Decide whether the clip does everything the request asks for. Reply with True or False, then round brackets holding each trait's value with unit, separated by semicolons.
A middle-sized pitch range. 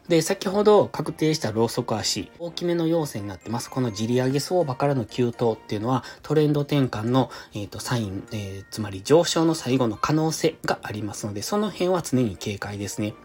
False (6.4 semitones)